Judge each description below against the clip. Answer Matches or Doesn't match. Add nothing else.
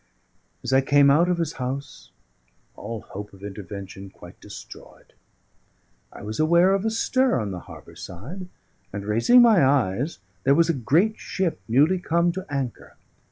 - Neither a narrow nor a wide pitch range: Doesn't match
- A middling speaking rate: Matches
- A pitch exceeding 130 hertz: Matches